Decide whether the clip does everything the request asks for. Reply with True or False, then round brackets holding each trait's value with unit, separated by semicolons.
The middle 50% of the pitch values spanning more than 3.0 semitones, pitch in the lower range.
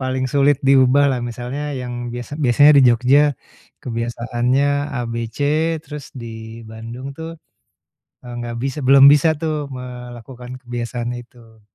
False (2.4 semitones; 125 Hz)